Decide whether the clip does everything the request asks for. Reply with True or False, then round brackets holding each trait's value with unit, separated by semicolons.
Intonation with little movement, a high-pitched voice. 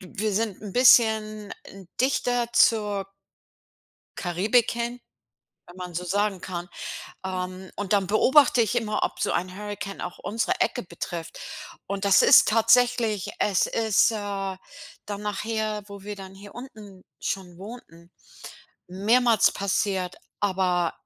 False (3.0 semitones; 205 Hz)